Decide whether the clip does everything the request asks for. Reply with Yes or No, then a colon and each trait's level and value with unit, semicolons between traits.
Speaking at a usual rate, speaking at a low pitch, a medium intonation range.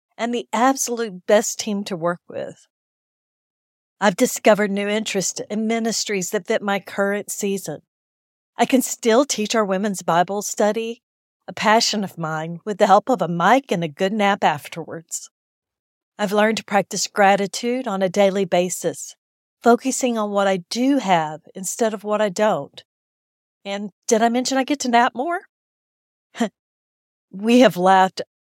No: average, 160 wpm; high, 210 Hz; average, 3.2 semitones